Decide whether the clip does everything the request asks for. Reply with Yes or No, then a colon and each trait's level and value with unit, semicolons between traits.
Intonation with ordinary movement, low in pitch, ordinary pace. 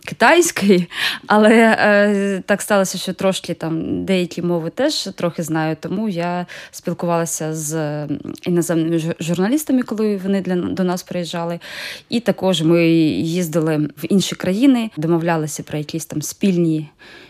No: average, 3.2 semitones; medium, 175 Hz; average, 130 wpm